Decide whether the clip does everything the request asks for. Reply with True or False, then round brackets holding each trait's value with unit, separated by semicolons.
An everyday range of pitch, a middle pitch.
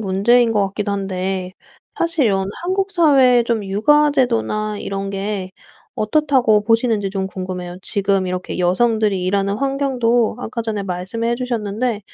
False (4.0 semitones; 215 Hz)